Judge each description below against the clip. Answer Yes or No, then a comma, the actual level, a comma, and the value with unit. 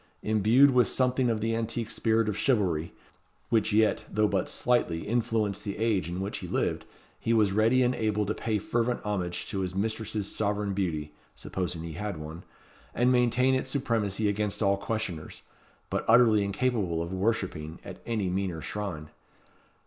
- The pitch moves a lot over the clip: No, average, 3.3 semitones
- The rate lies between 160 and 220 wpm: Yes, average, 165 wpm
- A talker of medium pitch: No, low, 105 Hz